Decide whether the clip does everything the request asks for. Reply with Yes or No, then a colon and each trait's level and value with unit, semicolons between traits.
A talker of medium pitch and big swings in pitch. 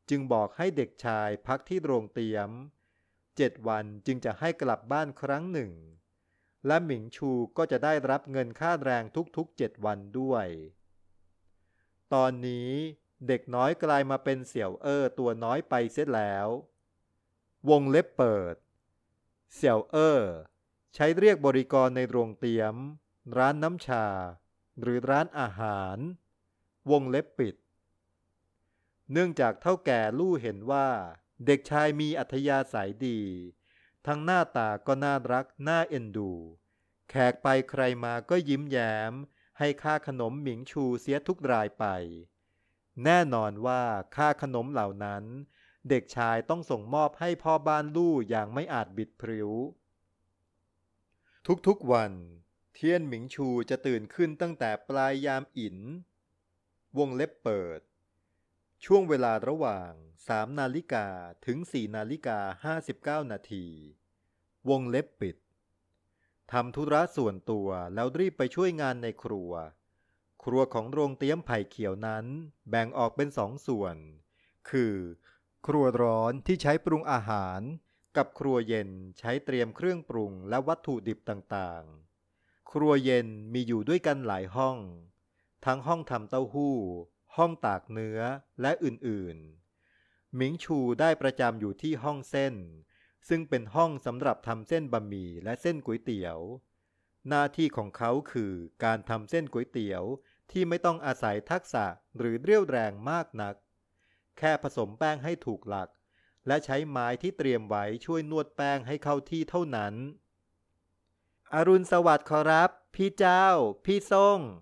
No: low, 120 Hz; wide, 6.7 semitones